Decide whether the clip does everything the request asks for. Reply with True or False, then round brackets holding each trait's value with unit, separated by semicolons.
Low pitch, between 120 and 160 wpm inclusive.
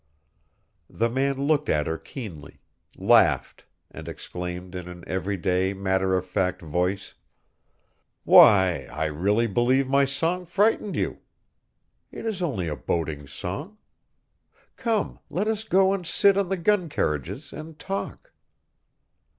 True (110 Hz; 135 wpm)